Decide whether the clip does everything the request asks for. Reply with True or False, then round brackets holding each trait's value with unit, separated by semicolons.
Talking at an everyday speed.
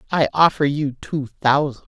True (155 wpm)